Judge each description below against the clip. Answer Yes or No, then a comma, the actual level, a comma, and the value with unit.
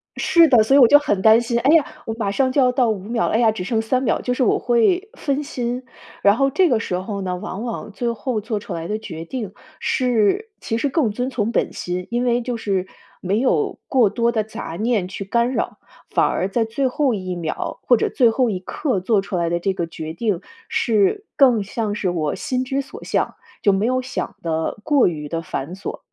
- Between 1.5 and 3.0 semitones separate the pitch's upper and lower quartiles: No, average, 4.6 semitones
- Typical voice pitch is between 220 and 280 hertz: Yes, high, 225 Hz